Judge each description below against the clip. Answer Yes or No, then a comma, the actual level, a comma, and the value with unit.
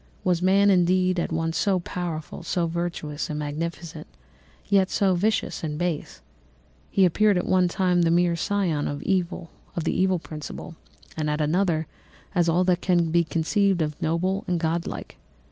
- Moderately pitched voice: Yes, medium, 175 Hz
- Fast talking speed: No, average, 160 wpm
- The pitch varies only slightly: Yes, narrow, 2.3 semitones